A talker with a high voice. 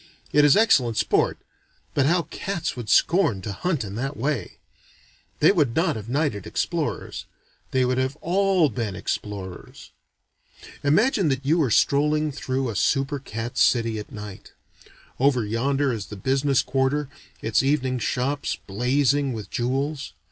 No: low, 135 Hz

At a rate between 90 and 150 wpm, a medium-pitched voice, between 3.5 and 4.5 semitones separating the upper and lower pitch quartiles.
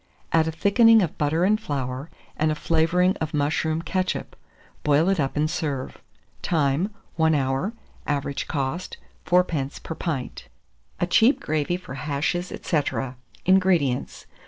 Yes: average, 140 wpm; medium, 160 Hz; average, 4.0 semitones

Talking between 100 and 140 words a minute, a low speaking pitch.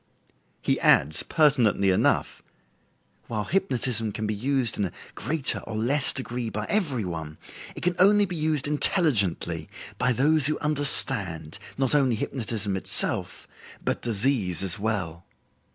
Yes: slow, 135 wpm; low, 120 Hz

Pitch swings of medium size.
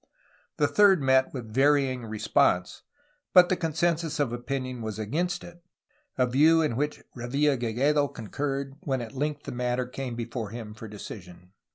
Yes: average, 4.0 semitones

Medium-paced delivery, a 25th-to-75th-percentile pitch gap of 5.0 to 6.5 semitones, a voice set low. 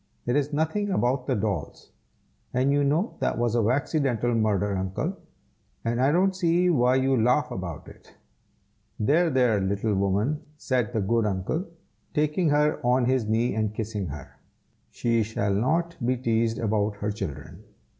Yes: average, 160 wpm; wide, 5.4 semitones; low, 120 Hz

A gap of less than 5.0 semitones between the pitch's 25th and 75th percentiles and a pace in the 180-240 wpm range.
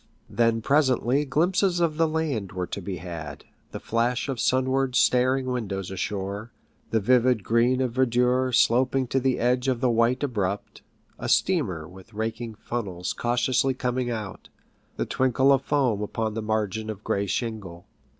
No: average, 3.7 semitones; average, 160 wpm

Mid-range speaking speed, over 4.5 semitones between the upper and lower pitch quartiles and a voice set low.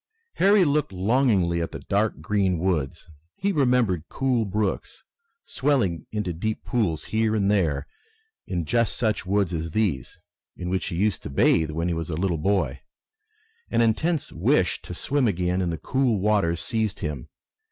Yes: average, 165 wpm; average, 5.0 semitones; low, 100 Hz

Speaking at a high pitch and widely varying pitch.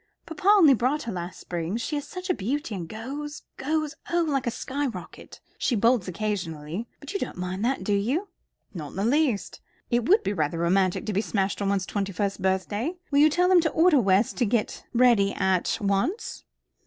Yes: high, 225 Hz; wide, 7.4 semitones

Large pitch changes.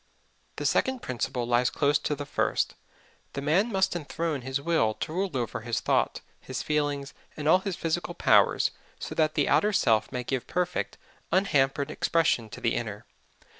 No: average, 4.8 semitones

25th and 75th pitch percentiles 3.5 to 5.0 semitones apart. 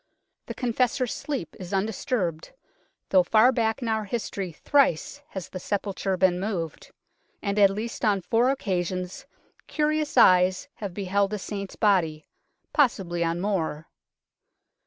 Yes: average, 4.0 semitones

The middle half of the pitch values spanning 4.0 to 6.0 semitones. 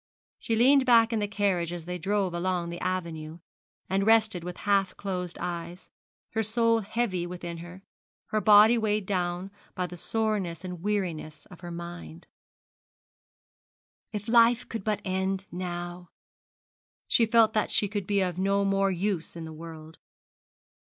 No: average, 3.3 semitones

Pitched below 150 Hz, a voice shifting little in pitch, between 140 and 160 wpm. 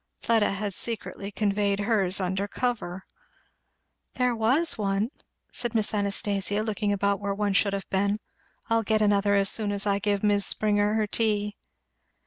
No: high, 205 Hz; narrow, 1.4 semitones; average, 155 wpm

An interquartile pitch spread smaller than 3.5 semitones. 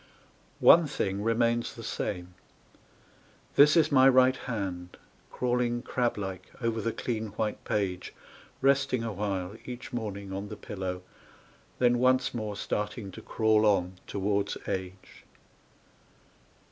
No: average, 3.9 semitones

